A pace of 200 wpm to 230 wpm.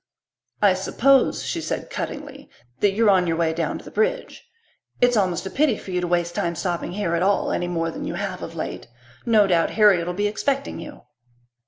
Yes: fast, 205 wpm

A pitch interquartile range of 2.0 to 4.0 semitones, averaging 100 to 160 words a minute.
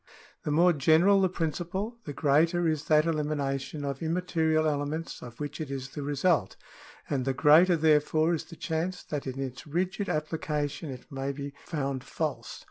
No: average, 3.0 semitones; average, 175 wpm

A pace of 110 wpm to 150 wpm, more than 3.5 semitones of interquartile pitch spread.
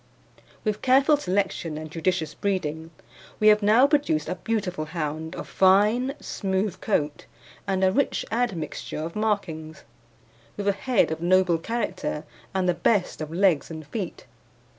Yes: average, 145 wpm; average, 4.9 semitones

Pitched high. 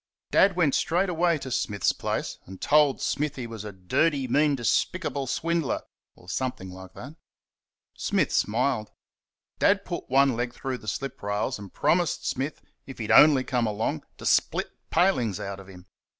No: low, 130 Hz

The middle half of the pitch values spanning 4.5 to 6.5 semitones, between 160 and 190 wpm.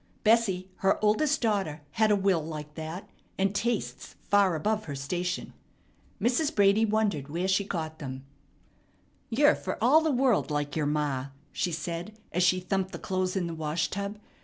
Yes: average, 5.1 semitones; average, 170 wpm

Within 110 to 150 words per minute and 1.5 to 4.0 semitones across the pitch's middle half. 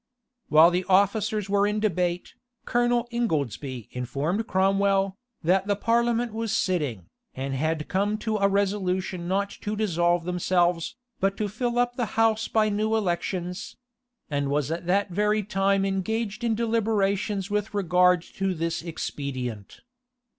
Yes: average, 140 wpm; average, 3.7 semitones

